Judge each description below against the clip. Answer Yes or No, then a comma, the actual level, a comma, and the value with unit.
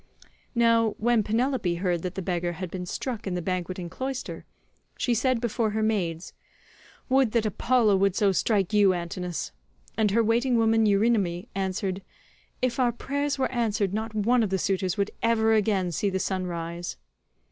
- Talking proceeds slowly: No, average, 170 wpm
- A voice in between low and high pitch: No, high, 205 Hz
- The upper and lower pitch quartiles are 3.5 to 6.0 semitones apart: Yes, average, 3.9 semitones